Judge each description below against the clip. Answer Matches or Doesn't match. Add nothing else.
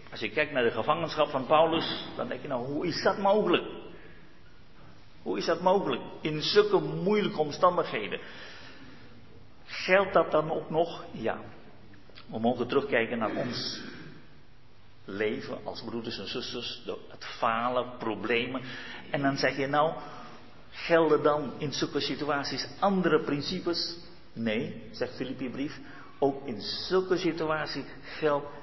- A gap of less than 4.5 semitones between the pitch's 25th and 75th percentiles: Doesn't match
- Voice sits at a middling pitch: Matches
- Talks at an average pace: Doesn't match